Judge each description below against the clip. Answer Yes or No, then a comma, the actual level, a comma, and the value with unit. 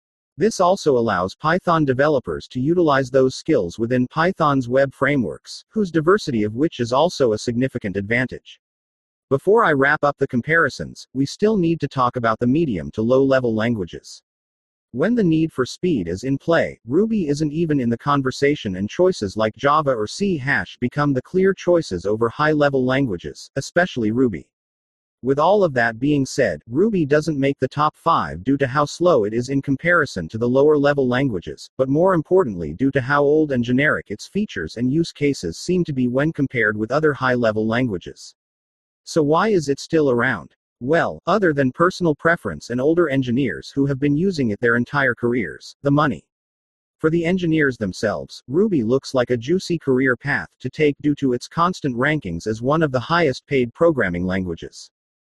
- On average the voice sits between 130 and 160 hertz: Yes, low, 135 Hz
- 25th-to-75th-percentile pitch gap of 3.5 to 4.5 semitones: No, average, 5.0 semitones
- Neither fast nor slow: Yes, average, 185 wpm